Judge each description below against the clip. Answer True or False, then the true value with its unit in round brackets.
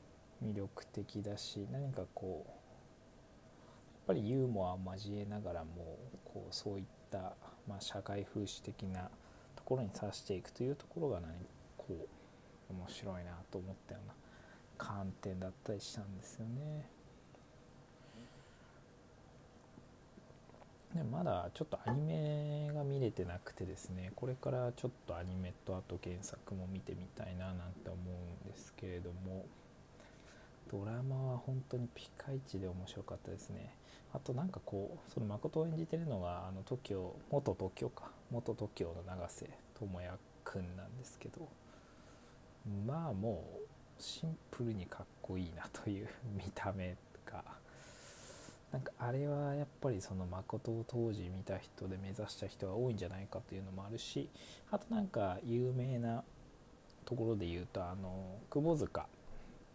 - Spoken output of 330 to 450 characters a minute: False (285 characters per minute)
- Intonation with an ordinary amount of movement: True (5.0 semitones)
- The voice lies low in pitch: True (100 Hz)